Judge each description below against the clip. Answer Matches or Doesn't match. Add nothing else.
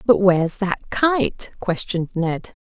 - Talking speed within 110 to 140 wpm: Matches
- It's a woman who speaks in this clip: Matches